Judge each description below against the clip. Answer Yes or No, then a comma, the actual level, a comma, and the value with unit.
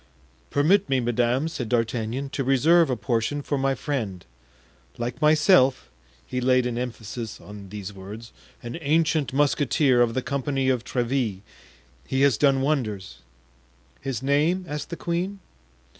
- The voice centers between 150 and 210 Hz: No, low, 130 Hz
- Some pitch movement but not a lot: Yes, average, 3.7 semitones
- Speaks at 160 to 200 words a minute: No, average, 145 wpm